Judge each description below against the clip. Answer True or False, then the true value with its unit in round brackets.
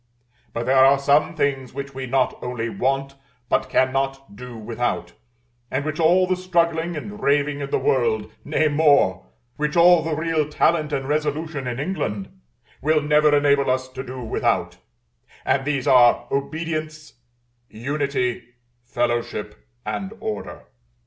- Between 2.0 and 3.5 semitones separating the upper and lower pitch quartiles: True (3.2 semitones)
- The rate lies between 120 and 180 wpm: True (140 wpm)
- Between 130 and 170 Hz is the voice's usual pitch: True (140 Hz)